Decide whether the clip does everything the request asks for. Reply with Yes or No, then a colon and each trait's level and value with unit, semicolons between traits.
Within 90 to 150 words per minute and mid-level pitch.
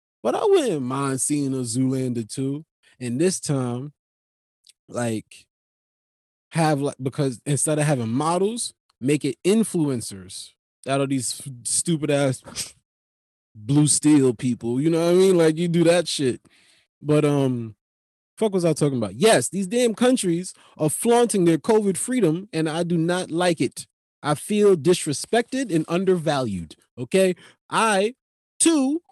Yes: average, 140 wpm; medium, 150 Hz